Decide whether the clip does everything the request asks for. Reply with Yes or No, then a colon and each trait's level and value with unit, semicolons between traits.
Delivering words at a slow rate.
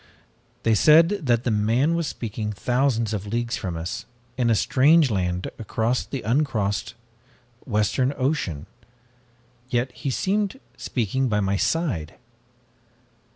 Yes: slow, 125 wpm